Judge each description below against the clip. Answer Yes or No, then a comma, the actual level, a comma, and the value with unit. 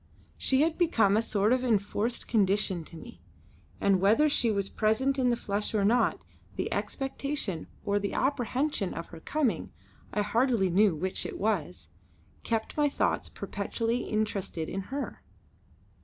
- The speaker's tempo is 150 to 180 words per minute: Yes, average, 155 wpm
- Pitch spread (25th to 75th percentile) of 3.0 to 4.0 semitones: No, average, 4.4 semitones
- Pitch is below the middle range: No, high, 215 Hz